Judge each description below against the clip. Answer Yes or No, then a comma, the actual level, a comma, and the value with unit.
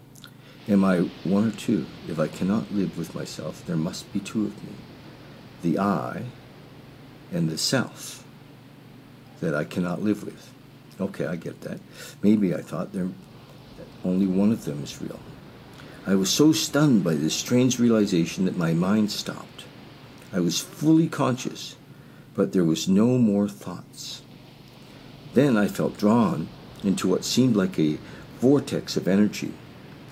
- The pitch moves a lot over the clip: Yes, wide, 6.4 semitones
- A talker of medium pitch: No, low, 110 Hz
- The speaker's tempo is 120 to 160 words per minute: Yes, average, 150 wpm